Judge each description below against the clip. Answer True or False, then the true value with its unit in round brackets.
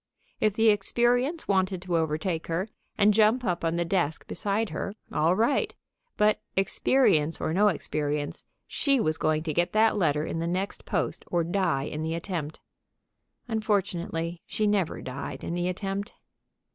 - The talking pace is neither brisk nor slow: True (160 wpm)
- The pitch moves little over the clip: False (4.5 semitones)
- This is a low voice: False (180 Hz)